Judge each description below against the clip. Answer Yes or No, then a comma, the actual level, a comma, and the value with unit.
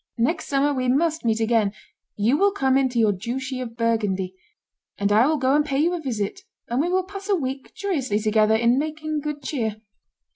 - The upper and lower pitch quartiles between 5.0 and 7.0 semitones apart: Yes, average, 5.3 semitones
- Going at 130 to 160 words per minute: No, fast, 205 wpm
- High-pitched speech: Yes, very high, 260 Hz